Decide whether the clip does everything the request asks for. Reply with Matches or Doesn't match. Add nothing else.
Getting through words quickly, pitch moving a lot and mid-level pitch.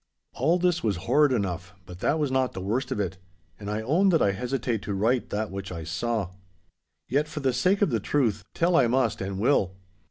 Doesn't match